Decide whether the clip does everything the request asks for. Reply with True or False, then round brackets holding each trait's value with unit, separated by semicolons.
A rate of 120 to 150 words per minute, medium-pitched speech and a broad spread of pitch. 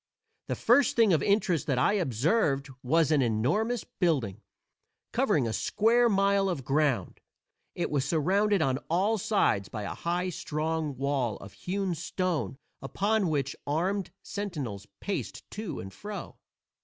True (145 wpm; 165 Hz; 6.7 semitones)